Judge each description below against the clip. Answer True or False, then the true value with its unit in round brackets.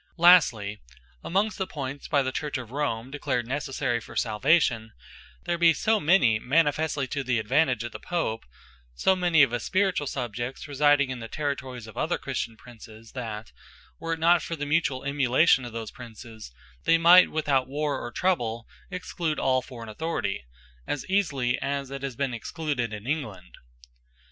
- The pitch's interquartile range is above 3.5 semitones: True (5.0 semitones)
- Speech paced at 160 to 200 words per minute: True (165 wpm)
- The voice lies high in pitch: False (135 Hz)